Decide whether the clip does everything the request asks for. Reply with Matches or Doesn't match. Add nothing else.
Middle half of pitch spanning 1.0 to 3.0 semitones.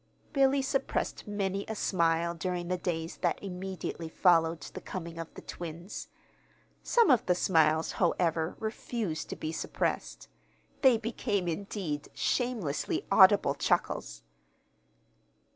Doesn't match